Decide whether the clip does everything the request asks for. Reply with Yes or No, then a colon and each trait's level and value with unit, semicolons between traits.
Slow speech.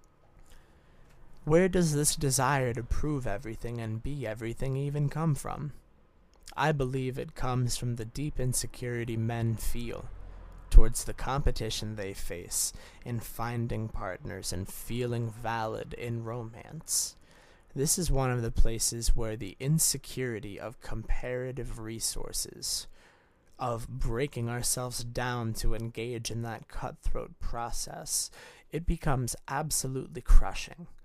Yes: slow, 120 wpm